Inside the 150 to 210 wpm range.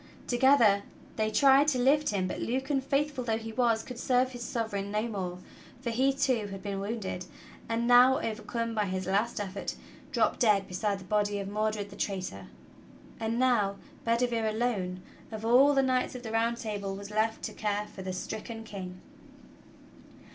Yes: average, 180 wpm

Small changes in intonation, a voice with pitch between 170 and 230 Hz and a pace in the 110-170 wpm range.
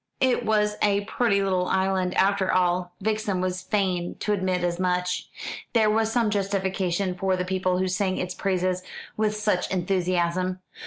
Yes: narrow, 1.9 semitones; medium, 185 Hz; average, 160 wpm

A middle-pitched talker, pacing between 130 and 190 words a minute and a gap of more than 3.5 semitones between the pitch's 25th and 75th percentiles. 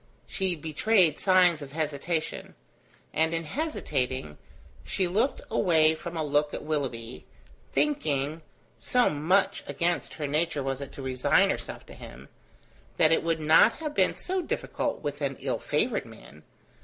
Yes: medium, 155 Hz; average, 150 wpm; average, 4.1 semitones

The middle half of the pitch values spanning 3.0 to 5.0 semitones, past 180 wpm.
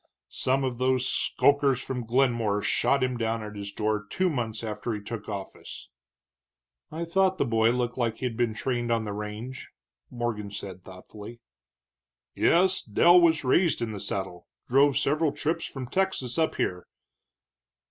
No: average, 4.4 semitones; average, 160 wpm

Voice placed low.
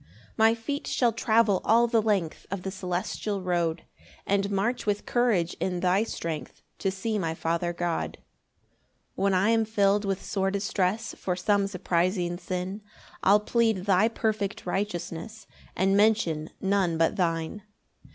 No: high, 195 Hz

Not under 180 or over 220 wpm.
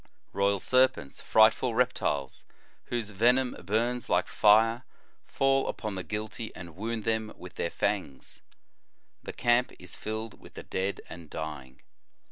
No: average, 140 wpm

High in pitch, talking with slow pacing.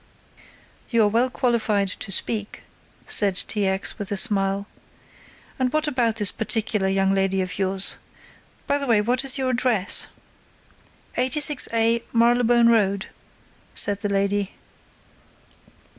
Yes: high, 215 Hz; slow, 130 wpm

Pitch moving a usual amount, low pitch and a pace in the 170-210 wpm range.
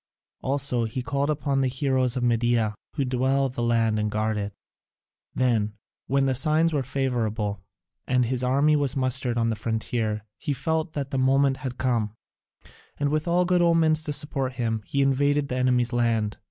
Yes: average, 3.1 semitones; low, 130 Hz; average, 180 wpm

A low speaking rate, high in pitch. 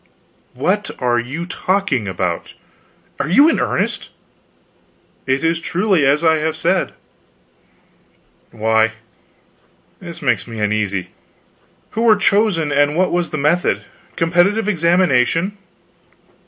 No: slow, 115 wpm; medium, 160 Hz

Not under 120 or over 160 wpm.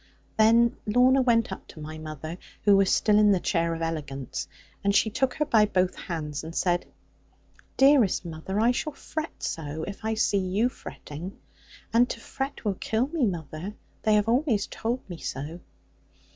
No: average, 175 wpm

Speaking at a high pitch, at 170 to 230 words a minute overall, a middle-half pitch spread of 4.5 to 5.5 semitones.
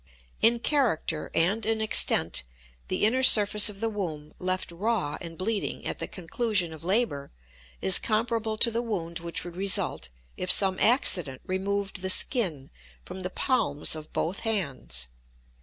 No: high, 195 Hz; average, 155 wpm; average, 5.1 semitones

